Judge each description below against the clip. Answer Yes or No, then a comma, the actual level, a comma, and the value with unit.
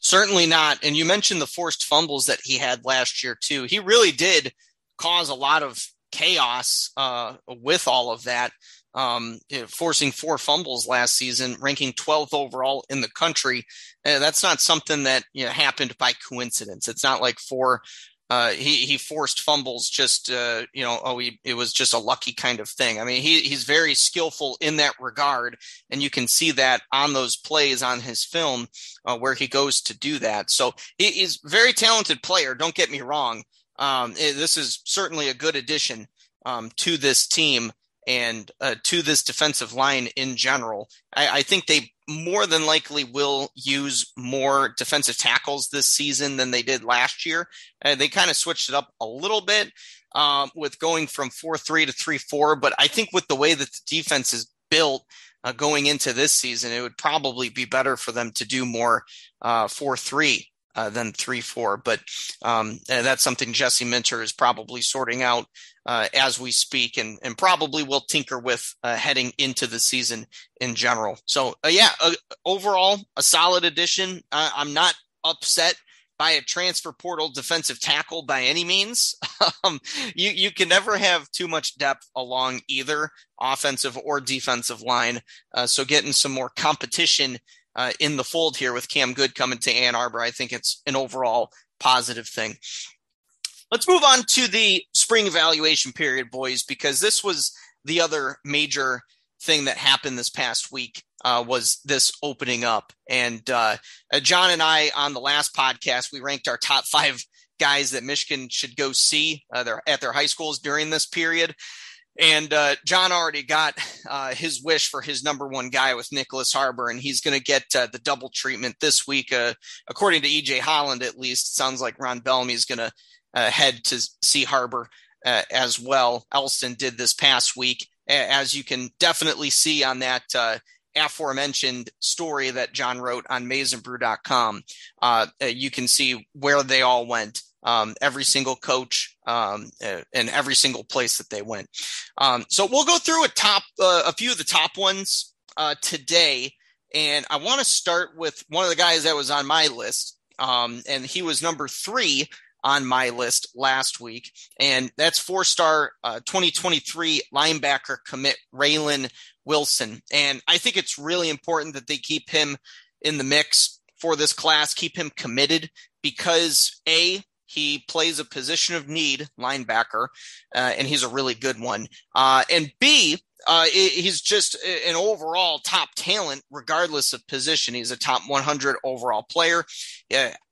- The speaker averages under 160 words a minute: No, average, 180 wpm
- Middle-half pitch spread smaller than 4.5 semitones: Yes, average, 3.9 semitones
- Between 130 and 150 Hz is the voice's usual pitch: Yes, medium, 140 Hz